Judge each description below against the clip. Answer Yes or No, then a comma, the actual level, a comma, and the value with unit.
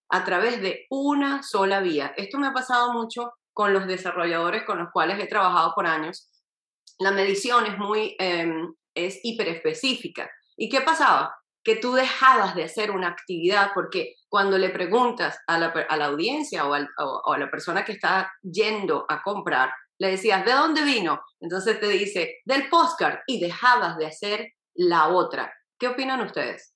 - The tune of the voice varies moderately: No, wide, 6.8 semitones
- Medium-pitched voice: No, high, 210 Hz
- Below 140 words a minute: No, average, 175 wpm